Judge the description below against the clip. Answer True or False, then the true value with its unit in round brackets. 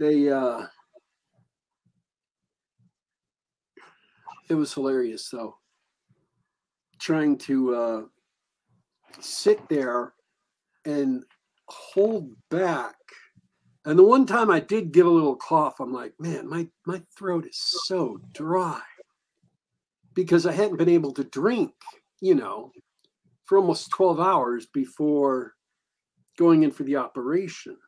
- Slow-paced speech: True (110 wpm)